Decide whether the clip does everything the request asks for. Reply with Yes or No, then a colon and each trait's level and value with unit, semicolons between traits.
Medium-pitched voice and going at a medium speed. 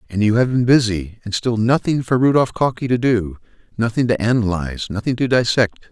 No: low, 115 Hz; average, 195 wpm